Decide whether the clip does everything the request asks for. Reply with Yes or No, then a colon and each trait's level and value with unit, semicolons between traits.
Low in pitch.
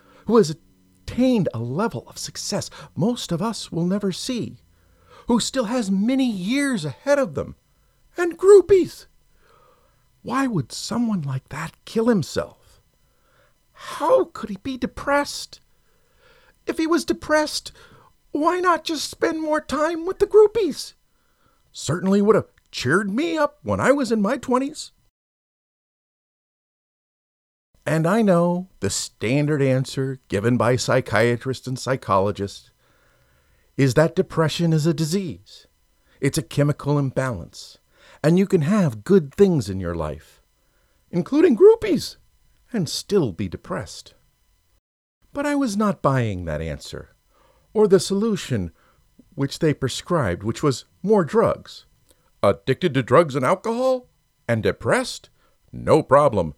No: medium, 175 Hz